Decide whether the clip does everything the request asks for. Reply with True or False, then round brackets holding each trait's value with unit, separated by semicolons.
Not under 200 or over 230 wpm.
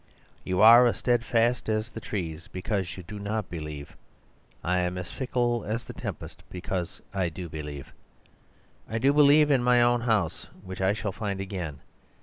False (165 wpm)